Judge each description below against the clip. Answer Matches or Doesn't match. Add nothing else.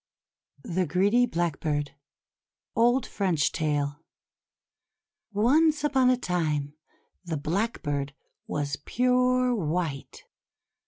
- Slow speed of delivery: Matches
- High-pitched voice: Doesn't match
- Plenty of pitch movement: Matches